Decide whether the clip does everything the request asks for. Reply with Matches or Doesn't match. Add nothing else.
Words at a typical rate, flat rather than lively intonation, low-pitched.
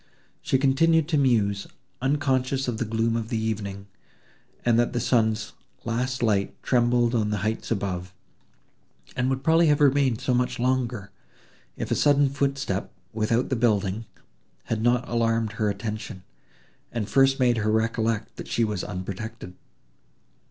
Doesn't match